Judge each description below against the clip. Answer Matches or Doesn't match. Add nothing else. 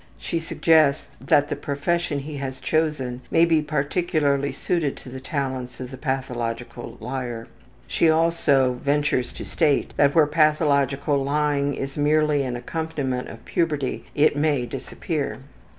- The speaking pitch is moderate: Matches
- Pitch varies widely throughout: Doesn't match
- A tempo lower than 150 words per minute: Matches